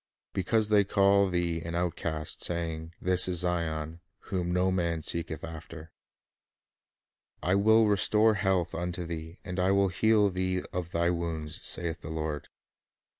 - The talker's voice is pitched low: Yes, very low, 90 Hz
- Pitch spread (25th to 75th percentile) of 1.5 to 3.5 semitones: Yes, narrow, 2.6 semitones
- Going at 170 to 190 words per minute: No, average, 145 wpm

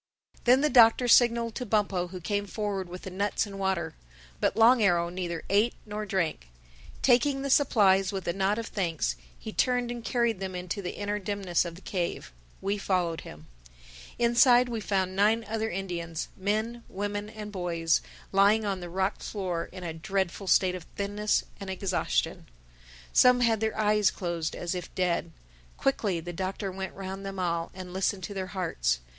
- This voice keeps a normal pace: Yes, average, 180 wpm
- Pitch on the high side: Yes, high, 195 Hz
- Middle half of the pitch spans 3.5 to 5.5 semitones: No, average, 3.1 semitones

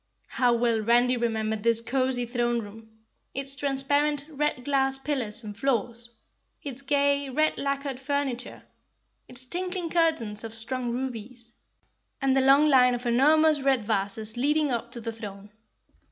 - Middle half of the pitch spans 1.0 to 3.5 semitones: Yes, average, 3.2 semitones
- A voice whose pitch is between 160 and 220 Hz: No, very high, 255 Hz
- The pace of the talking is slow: No, average, 145 wpm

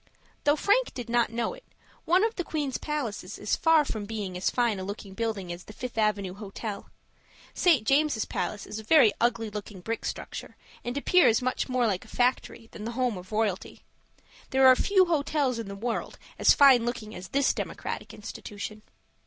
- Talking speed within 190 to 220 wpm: Yes, average, 195 wpm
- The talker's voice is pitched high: Yes, high, 230 Hz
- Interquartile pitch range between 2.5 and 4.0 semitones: No, average, 4.9 semitones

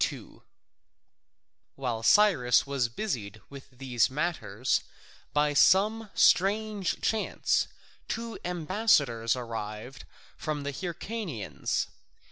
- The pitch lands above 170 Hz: No, medium, 140 Hz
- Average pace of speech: No, slow, 90 wpm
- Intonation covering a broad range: Yes, wide, 8.6 semitones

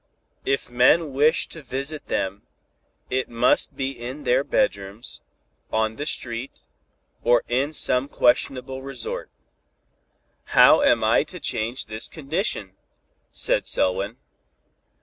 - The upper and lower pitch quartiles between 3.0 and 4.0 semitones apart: Yes, average, 3.4 semitones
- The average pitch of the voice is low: Yes, low, 125 Hz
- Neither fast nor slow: No, slow, 120 wpm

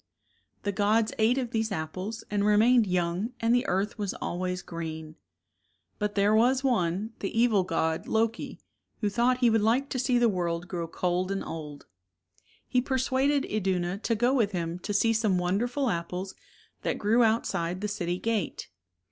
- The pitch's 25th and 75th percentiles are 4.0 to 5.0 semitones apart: Yes, average, 4.4 semitones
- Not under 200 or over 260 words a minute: No, average, 170 wpm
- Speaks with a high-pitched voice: Yes, high, 210 Hz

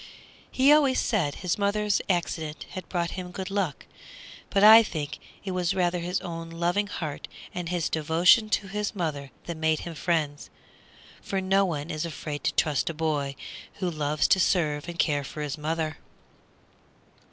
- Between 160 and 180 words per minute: Yes, average, 170 wpm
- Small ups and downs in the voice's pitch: No, average, 3.7 semitones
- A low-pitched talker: No, medium, 170 Hz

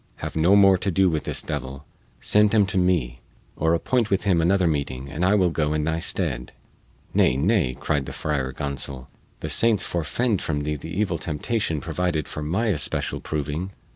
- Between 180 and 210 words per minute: Yes, average, 190 wpm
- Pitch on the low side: Yes, very low, 80 Hz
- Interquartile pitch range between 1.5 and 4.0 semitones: No, average, 4.8 semitones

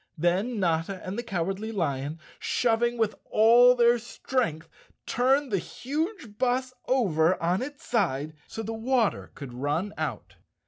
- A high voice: Yes, high, 215 Hz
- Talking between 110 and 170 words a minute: Yes, average, 140 wpm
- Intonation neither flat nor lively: No, wide, 6.7 semitones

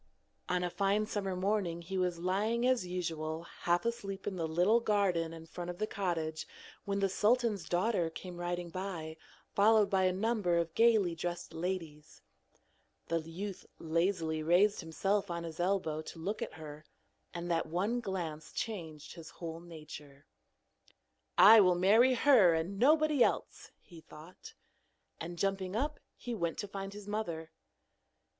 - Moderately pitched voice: Yes, medium, 180 Hz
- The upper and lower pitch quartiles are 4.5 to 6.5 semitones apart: No, average, 3.7 semitones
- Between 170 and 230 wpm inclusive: No, average, 155 wpm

